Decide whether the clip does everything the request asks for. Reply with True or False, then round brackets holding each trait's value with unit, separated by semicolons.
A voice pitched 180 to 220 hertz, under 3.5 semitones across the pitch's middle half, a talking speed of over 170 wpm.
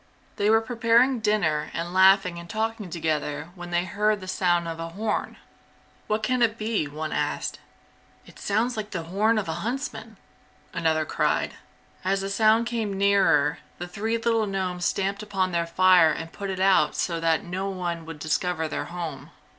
False (190 Hz; 4.1 semitones; 180 wpm)